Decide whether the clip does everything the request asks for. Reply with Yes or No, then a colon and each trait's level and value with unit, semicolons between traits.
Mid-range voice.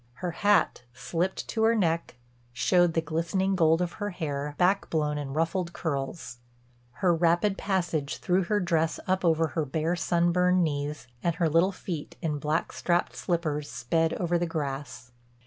Yes: medium, 170 Hz